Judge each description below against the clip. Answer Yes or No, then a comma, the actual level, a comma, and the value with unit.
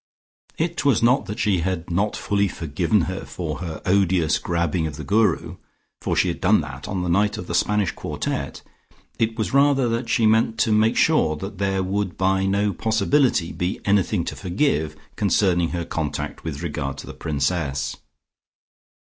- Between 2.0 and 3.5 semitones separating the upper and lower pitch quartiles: No, average, 4.3 semitones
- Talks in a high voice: No, very low, 95 Hz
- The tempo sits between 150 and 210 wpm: Yes, average, 175 wpm